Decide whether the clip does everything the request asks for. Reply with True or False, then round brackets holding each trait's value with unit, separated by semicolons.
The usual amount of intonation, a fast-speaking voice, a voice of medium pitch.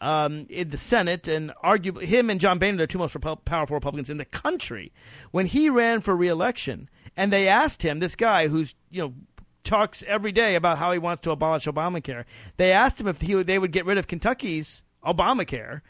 True (4.2 semitones; 215 wpm; 175 Hz)